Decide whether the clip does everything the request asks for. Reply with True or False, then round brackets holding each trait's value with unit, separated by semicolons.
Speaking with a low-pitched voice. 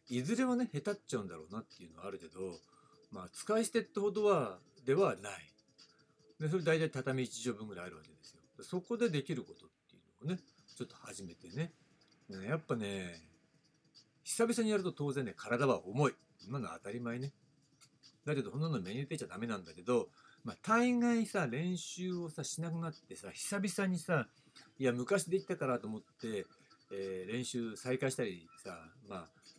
False (155 Hz)